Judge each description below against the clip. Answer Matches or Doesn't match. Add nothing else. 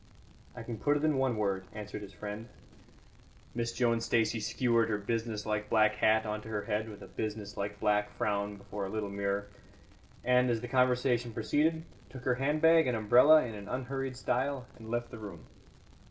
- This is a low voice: Matches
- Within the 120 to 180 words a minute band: Doesn't match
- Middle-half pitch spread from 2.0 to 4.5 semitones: Matches